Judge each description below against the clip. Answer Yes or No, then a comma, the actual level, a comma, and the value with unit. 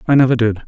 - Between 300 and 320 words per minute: No, fast, 270 wpm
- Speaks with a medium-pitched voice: No, low, 120 Hz